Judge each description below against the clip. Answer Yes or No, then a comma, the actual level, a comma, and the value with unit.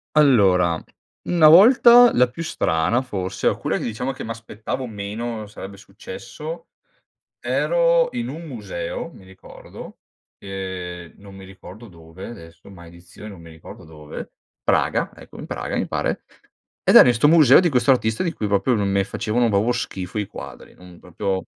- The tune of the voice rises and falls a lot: Yes, wide, 5.7 semitones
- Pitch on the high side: No, low, 105 Hz